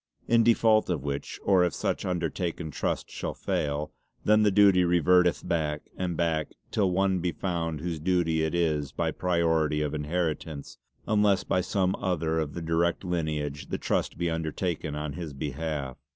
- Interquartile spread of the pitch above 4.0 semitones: No, average, 2.9 semitones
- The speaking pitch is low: Yes, very low, 85 Hz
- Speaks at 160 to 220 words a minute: Yes, average, 165 wpm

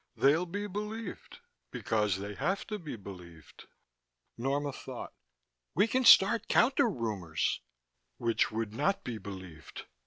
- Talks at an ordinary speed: No, slow, 125 wpm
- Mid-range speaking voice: No, low, 130 Hz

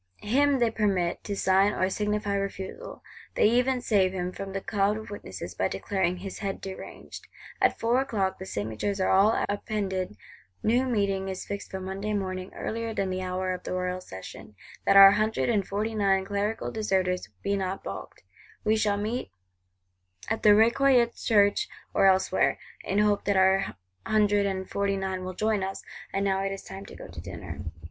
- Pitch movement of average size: No, narrow, 2.0 semitones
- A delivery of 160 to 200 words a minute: Yes, average, 180 wpm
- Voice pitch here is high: Yes, high, 195 Hz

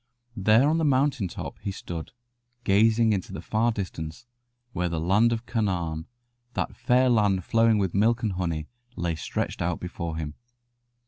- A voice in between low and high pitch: No, low, 100 Hz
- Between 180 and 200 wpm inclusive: No, average, 160 wpm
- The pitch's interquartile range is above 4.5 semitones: Yes, average, 5.0 semitones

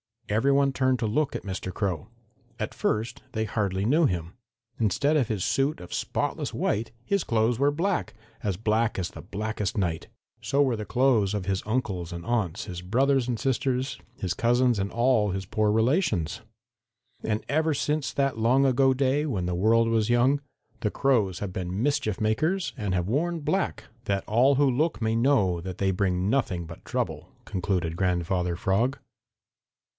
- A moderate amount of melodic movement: No, wide, 5.8 semitones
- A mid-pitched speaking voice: No, low, 110 Hz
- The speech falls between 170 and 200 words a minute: Yes, average, 175 wpm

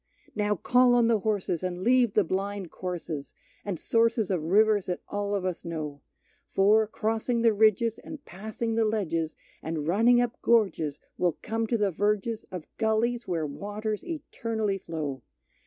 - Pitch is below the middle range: No, high, 210 Hz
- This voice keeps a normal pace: Yes, average, 160 wpm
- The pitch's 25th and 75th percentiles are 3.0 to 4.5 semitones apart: Yes, average, 4.1 semitones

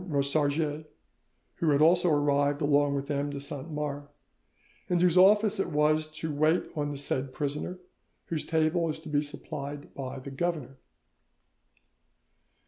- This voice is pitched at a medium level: Yes, medium, 150 Hz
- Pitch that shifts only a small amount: Yes, narrow, 2.0 semitones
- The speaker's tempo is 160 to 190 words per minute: No, average, 145 wpm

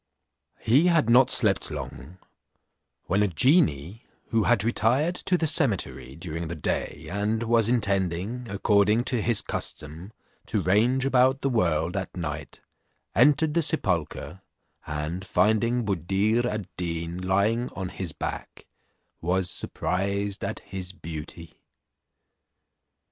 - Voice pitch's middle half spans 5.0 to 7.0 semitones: Yes, wide, 5.5 semitones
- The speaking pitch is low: Yes, low, 100 Hz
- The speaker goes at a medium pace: No, slow, 125 wpm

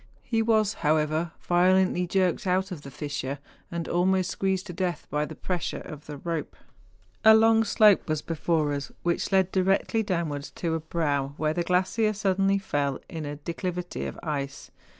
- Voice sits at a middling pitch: Yes, medium, 175 Hz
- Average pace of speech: Yes, average, 170 wpm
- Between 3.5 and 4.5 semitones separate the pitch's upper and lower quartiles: Yes, average, 3.9 semitones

